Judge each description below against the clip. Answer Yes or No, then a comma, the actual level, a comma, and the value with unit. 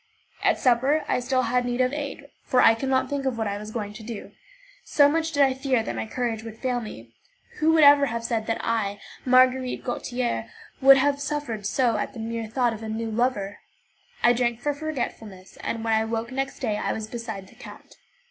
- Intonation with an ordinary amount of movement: Yes, average, 3.2 semitones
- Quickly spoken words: Yes, fast, 220 wpm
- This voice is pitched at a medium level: No, high, 240 Hz